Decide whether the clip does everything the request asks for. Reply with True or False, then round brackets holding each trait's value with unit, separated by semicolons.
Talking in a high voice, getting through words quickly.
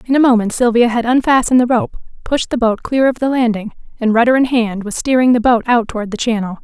True (235 Hz; 245 wpm)